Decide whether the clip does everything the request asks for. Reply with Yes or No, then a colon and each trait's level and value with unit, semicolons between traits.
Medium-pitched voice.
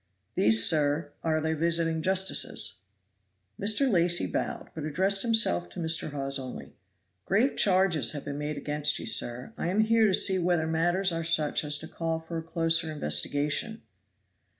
Yes: medium, 160 Hz